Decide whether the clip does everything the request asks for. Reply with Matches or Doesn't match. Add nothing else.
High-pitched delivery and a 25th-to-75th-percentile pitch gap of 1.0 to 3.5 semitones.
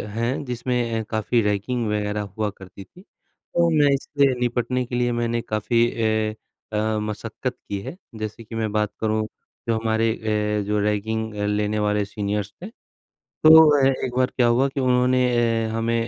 Doesn't match